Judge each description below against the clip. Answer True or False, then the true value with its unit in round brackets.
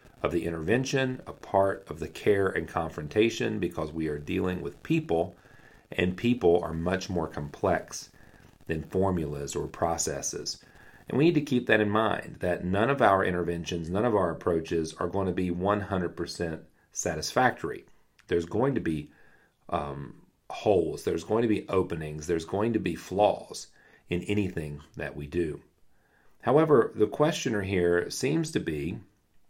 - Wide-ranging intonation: False (4.5 semitones)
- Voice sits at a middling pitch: False (90 Hz)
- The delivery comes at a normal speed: True (155 wpm)